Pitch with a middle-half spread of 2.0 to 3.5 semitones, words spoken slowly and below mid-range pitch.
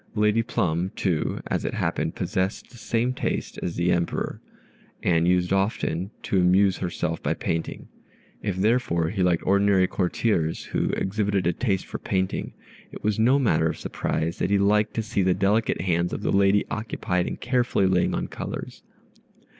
No: average, 3.2 semitones; average, 170 wpm; very low, 95 Hz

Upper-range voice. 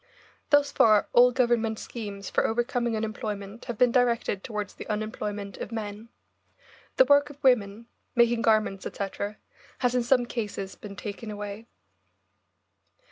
Yes: high, 225 Hz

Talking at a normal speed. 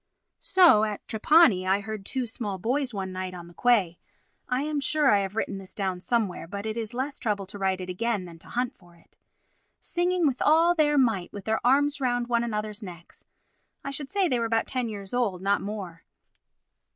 No: fast, 210 wpm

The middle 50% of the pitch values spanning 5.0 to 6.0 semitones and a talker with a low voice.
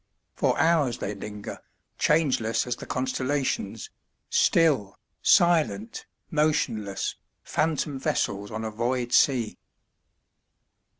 Yes: wide, 5.6 semitones; low, 125 Hz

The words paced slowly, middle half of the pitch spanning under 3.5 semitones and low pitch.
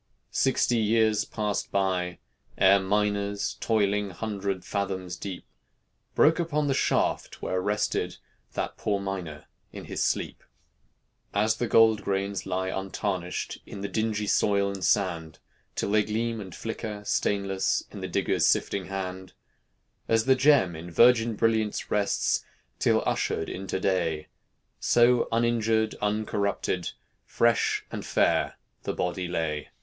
Yes: slow, 130 wpm; average, 2.8 semitones; low, 100 Hz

